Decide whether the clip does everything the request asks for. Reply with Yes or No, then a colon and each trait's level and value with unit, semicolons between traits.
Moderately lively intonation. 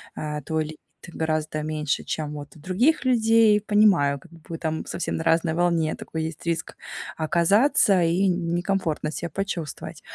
Yes: average, 3.7 semitones